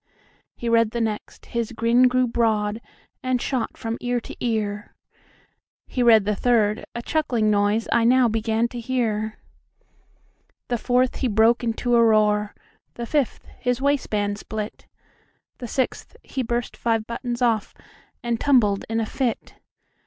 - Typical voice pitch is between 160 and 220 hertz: No, high, 230 Hz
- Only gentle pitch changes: Yes, narrow, 2.2 semitones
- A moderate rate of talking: No, slow, 130 wpm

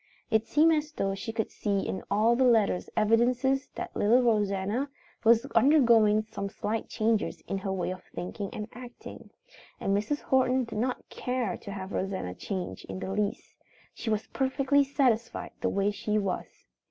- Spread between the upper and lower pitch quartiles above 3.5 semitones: Yes, average, 3.9 semitones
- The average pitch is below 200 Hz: No, high, 220 Hz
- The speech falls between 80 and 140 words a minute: No, average, 170 wpm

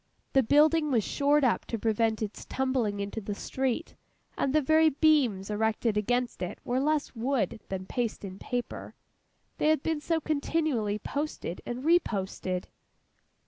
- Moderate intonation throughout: No, wide, 5.9 semitones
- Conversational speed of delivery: Yes, average, 150 wpm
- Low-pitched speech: No, high, 245 Hz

